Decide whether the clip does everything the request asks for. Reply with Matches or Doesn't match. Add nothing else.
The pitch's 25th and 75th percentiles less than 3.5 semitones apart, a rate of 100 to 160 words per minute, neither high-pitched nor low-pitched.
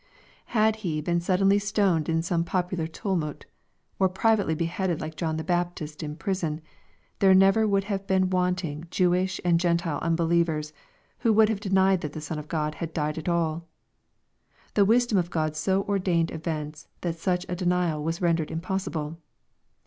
Doesn't match